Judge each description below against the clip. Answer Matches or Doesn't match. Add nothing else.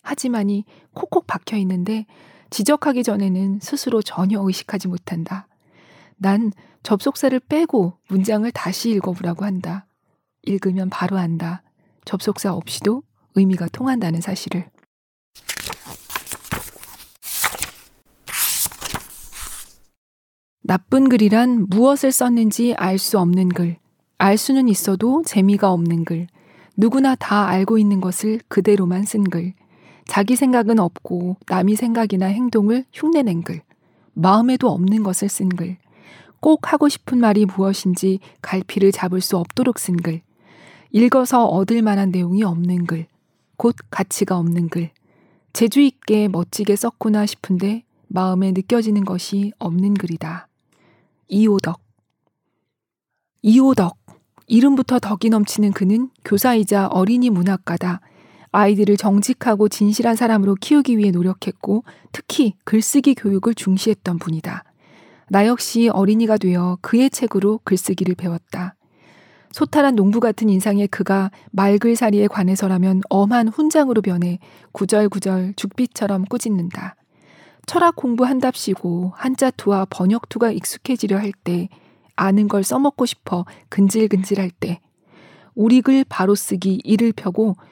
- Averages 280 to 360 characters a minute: Doesn't match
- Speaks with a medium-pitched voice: Doesn't match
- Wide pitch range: Doesn't match